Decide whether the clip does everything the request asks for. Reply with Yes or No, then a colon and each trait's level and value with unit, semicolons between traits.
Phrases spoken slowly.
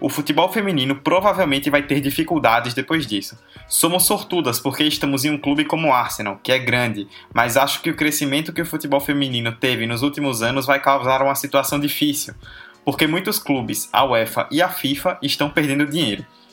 No: fast, 185 wpm